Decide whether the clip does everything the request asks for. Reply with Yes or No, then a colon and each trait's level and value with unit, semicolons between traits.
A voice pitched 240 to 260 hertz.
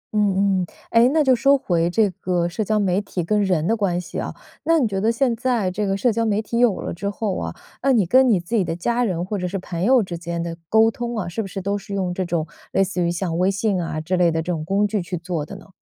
No: high, 195 Hz